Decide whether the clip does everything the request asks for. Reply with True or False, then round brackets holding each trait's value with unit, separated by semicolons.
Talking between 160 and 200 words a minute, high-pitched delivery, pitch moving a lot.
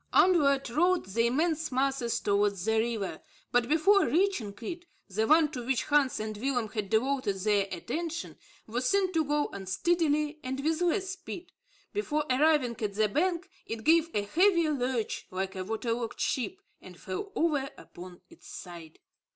True (165 wpm; 265 Hz; 7.0 semitones)